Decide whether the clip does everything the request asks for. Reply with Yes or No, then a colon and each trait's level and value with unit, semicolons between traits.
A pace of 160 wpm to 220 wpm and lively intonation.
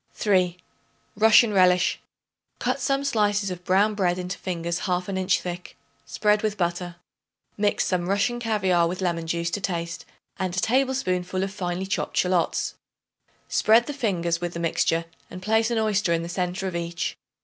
No: average, 170 wpm; average, 3.1 semitones